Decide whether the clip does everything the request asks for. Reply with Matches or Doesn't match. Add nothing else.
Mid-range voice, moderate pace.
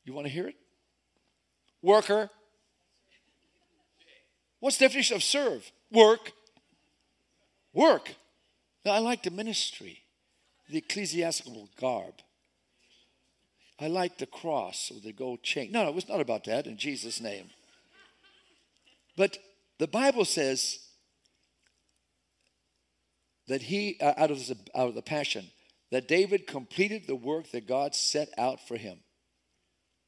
Doesn't match